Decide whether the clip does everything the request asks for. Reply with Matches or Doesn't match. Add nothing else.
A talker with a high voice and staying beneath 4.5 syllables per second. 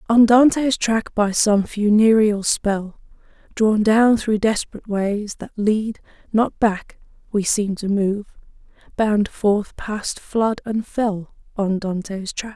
Matches